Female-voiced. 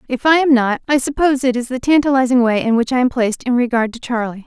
Yes: female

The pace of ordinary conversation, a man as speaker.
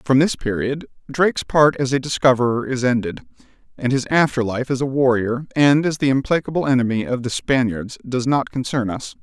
Yes: average, 190 wpm; male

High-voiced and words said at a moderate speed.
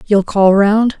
Yes: high, 205 Hz; average, 180 wpm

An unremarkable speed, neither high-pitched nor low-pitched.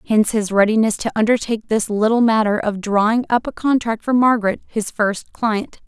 No: average, 185 wpm; high, 220 Hz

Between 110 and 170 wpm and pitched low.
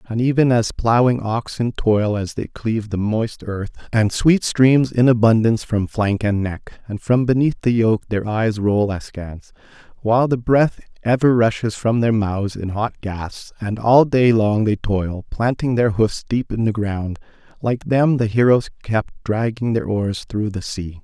No: average, 185 wpm; low, 110 Hz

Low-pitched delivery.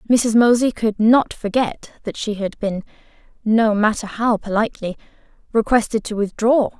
No: high, 220 Hz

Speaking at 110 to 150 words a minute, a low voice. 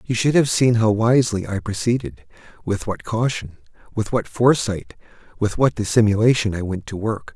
Yes: average, 145 wpm; low, 110 Hz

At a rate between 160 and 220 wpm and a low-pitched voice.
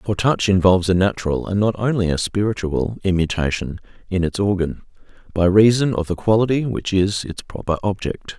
Yes: average, 170 wpm; very low, 95 Hz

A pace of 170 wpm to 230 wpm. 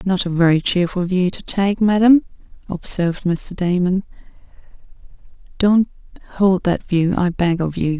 No: average, 145 wpm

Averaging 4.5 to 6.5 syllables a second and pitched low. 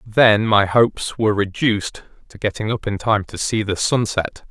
Yes: 4.8 syllables/s; low, 105 Hz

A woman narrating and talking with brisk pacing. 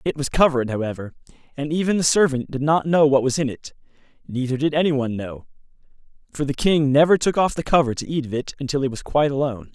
No: male; fast, 220 wpm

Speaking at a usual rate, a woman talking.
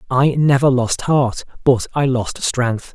No: average, 165 wpm; male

